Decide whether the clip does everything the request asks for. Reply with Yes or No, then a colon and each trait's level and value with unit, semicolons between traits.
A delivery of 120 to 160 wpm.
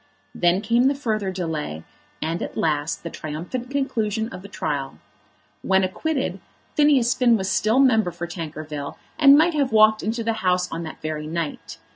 No: average, 170 wpm